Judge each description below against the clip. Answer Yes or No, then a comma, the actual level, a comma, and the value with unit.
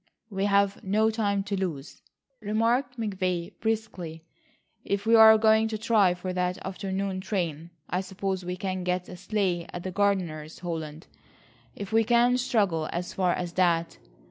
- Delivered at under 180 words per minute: Yes, average, 155 wpm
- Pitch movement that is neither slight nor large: Yes, average, 3.3 semitones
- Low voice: No, high, 190 Hz